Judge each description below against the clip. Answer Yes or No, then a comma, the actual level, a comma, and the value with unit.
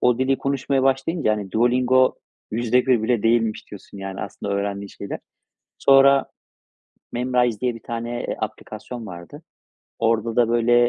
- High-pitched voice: No, low, 120 Hz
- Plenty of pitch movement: No, average, 2.9 semitones